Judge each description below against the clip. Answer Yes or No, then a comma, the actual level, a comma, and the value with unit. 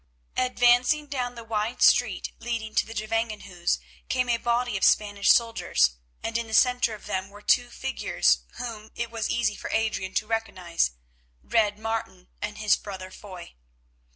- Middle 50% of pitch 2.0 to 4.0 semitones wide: Yes, average, 2.9 semitones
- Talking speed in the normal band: Yes, average, 155 wpm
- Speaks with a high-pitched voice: Yes, high, 220 Hz